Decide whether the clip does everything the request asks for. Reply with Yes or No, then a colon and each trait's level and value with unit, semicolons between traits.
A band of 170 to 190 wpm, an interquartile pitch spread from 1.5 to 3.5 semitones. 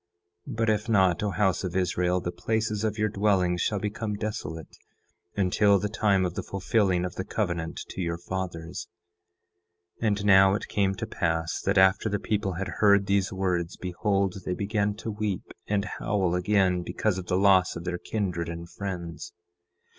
Yes: average, 180 wpm; average, 2.7 semitones